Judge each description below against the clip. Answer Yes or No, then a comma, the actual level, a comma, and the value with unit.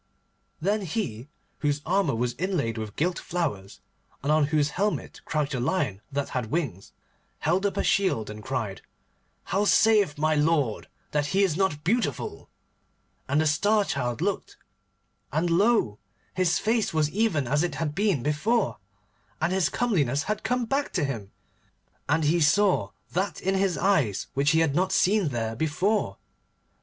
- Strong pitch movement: Yes, wide, 5.9 semitones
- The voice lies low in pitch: No, medium, 155 Hz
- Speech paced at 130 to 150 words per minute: No, average, 160 wpm